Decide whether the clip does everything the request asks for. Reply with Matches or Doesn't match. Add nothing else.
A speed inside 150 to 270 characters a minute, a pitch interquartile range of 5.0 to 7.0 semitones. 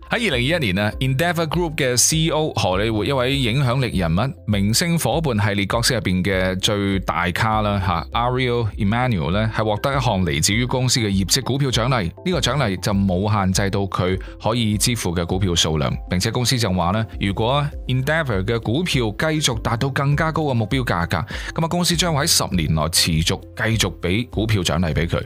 Doesn't match